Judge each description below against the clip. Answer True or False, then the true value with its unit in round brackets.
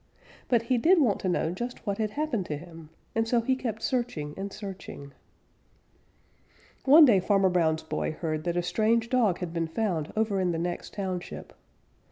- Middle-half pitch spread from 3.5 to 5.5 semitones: True (5.2 semitones)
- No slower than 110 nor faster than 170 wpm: False (185 wpm)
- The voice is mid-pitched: False (195 Hz)